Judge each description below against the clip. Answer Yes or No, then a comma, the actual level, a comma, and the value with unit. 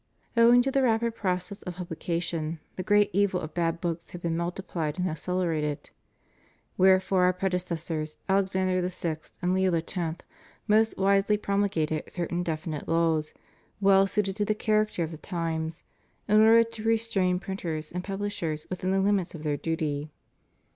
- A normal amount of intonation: Yes, average, 3.4 semitones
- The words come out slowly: No, average, 155 wpm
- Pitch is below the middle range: No, medium, 180 Hz